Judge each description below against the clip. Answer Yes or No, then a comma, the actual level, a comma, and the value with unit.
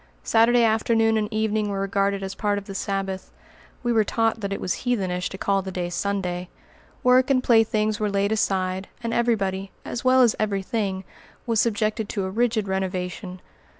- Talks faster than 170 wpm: Yes, average, 185 wpm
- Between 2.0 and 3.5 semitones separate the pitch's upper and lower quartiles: Yes, average, 2.7 semitones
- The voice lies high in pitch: Yes, high, 205 Hz